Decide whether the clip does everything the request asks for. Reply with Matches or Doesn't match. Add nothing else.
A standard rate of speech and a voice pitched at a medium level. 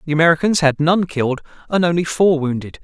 Matches